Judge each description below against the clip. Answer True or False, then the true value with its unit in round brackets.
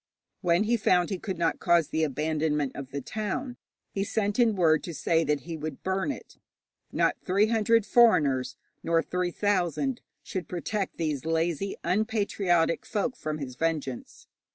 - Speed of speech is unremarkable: True (160 wpm)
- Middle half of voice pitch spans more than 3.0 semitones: True (4.7 semitones)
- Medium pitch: True (175 Hz)